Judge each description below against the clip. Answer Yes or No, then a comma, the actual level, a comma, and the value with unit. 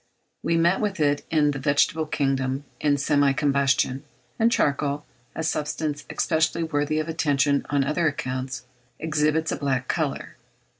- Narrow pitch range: Yes, narrow, 2.1 semitones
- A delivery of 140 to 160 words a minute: Yes, average, 145 wpm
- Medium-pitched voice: Yes, medium, 145 Hz